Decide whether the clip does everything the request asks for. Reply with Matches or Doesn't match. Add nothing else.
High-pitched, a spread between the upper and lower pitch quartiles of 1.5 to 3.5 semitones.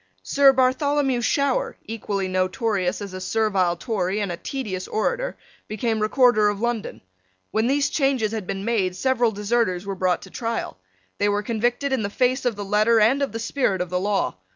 Doesn't match